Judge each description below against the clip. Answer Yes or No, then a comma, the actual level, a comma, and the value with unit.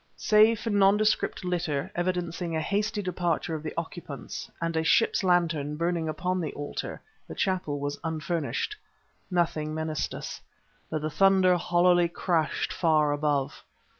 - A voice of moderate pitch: Yes, medium, 170 Hz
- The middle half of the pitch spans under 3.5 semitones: Yes, average, 2.9 semitones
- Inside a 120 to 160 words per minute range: Yes, average, 140 wpm